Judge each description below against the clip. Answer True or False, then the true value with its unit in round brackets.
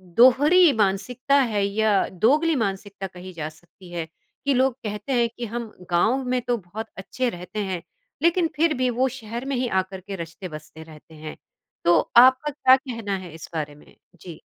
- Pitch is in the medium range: False (215 Hz)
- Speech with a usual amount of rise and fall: False (6.2 semitones)